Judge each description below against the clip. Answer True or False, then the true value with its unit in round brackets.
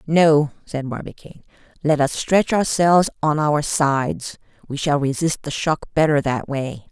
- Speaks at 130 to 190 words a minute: True (155 wpm)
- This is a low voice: False (150 Hz)